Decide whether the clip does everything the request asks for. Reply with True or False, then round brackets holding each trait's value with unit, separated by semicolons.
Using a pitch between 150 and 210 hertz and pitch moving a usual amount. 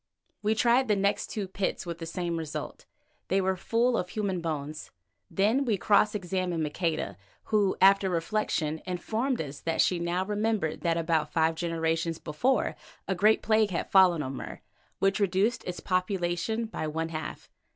True (185 Hz; 4.2 semitones)